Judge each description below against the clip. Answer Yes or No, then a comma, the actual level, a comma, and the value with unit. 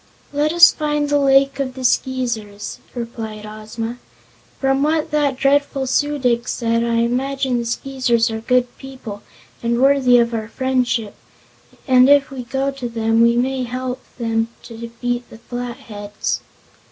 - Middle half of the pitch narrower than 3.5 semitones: Yes, average, 2.7 semitones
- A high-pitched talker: Yes, very high, 250 Hz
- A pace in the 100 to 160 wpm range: Yes, average, 155 wpm